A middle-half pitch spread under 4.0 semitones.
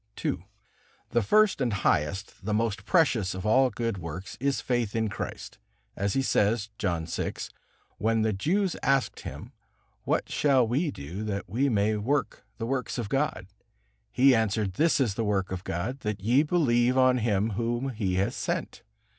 No: average, 4.7 semitones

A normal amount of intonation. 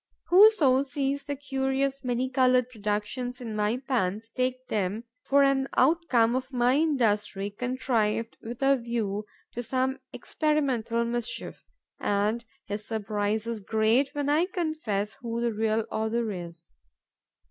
Yes: average, 3.8 semitones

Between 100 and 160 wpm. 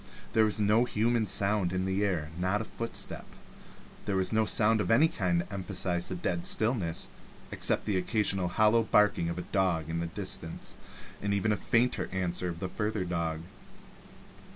No: average, 175 wpm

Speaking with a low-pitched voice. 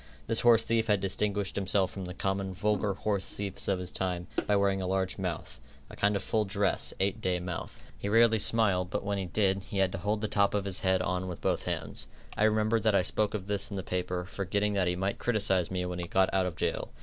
Yes: low, 100 Hz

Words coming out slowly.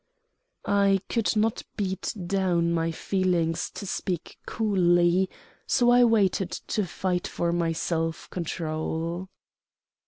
Yes: slow, 115 wpm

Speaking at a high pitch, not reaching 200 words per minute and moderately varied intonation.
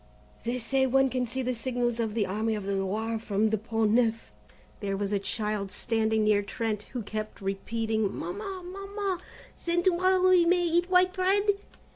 No: high, 230 Hz; average, 185 wpm; wide, 8.4 semitones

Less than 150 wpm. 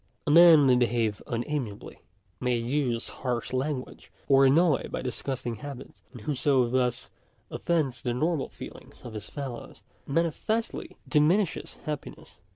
Yes: slow, 135 wpm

